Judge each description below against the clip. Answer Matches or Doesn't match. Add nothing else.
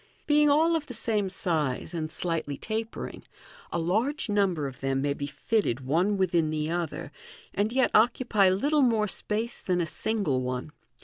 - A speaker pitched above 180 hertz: Matches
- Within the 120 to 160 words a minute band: Doesn't match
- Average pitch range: Doesn't match